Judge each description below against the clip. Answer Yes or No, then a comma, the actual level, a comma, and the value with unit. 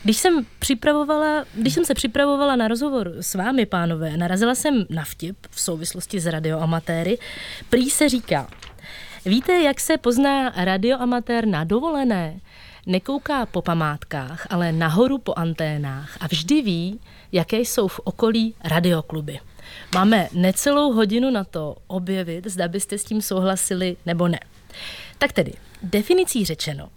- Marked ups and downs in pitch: Yes, wide, 6.6 semitones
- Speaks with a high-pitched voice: Yes, high, 195 Hz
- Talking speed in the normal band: Yes, average, 140 wpm